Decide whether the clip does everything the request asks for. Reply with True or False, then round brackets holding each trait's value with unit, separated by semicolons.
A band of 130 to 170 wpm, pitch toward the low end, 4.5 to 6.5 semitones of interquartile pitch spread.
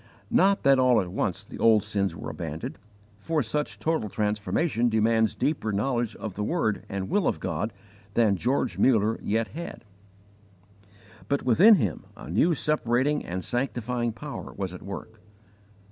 True (155 wpm; 115 Hz; 4.9 semitones)